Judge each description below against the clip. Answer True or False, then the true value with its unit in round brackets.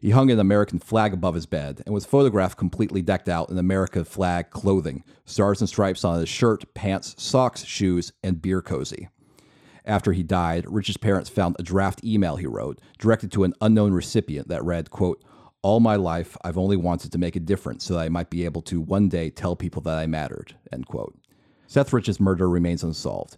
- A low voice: True (95 Hz)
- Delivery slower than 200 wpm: False (205 wpm)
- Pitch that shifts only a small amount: False (3.1 semitones)